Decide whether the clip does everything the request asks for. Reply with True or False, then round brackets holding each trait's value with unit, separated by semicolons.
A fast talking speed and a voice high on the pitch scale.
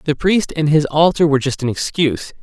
False (225 wpm; 150 Hz)